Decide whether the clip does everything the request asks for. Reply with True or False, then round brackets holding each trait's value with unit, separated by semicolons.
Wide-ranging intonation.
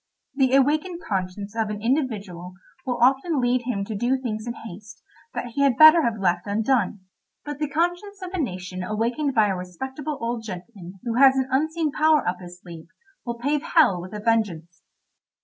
True (5.9 semitones)